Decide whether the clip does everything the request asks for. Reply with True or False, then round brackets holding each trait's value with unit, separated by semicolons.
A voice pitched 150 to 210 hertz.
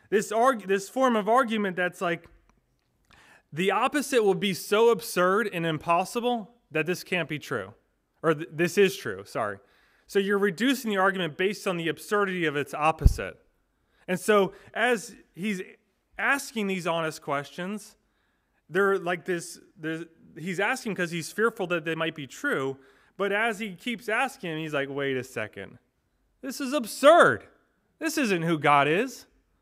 True (190 Hz)